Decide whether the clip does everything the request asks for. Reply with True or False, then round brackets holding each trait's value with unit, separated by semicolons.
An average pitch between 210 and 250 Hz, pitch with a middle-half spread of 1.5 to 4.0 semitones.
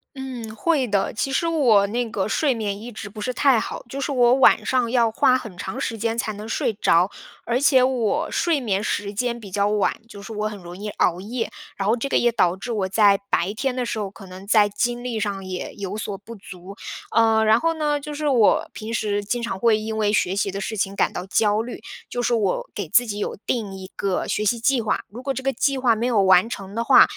True (220 Hz; 3.5 semitones)